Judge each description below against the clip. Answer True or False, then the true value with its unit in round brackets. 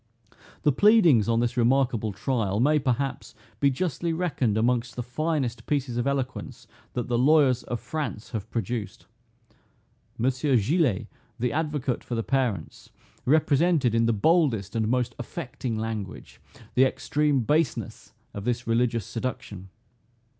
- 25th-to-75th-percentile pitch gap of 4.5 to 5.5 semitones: False (3.9 semitones)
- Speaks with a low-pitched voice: True (125 Hz)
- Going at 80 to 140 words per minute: True (135 wpm)